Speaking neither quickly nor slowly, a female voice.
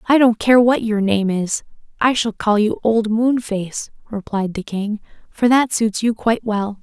Yes: average, 195 wpm; female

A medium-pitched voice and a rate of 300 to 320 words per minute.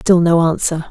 No: medium, 170 Hz; average, 200 wpm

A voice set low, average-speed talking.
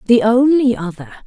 No: high, 230 Hz; average, 145 wpm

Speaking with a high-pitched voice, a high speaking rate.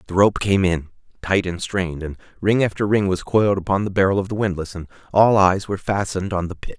No: very low, 95 Hz; fast, 240 wpm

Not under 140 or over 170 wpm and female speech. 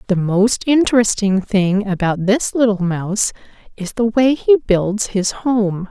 Yes: average, 150 wpm; female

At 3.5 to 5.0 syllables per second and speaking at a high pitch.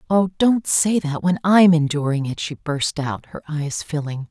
No: 4.3 syllables/s; medium, 160 Hz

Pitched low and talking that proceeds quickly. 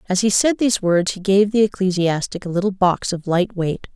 No: high, 190 Hz; fast, 230 wpm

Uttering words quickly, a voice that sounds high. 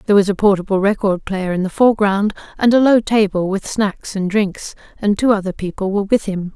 Yes: fast, 220 wpm; high, 200 Hz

